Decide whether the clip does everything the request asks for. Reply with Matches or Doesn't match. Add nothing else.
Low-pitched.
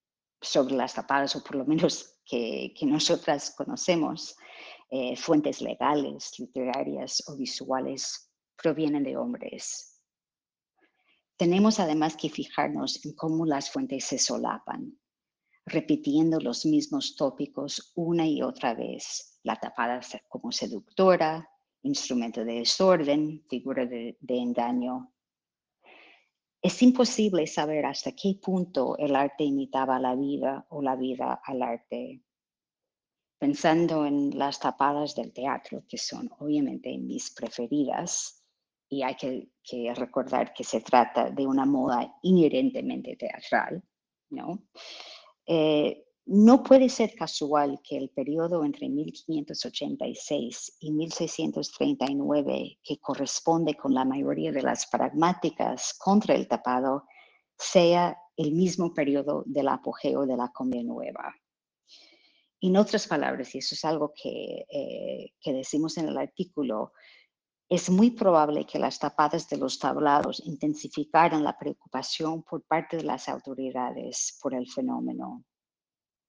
Doesn't match